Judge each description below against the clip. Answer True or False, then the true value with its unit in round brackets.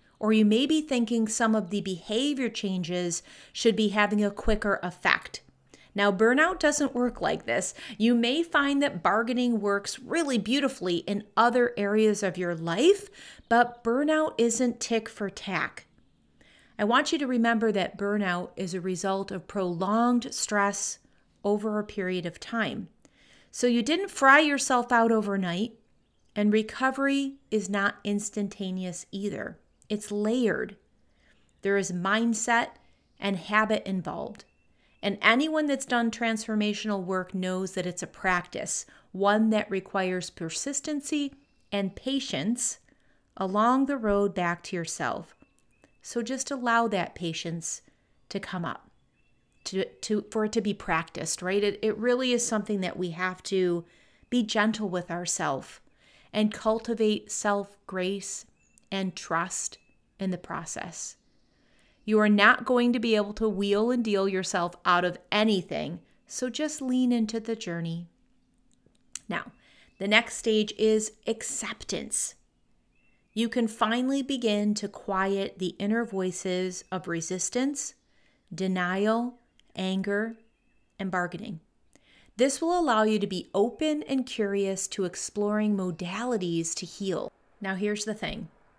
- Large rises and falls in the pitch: False (3.8 semitones)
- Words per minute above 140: False (135 wpm)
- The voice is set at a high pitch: True (210 Hz)